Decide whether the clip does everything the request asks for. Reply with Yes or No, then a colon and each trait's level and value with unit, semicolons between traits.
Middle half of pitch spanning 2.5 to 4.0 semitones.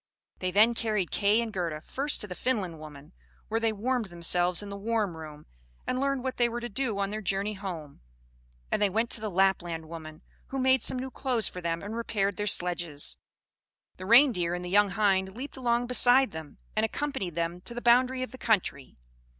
No: average, 5.2 semitones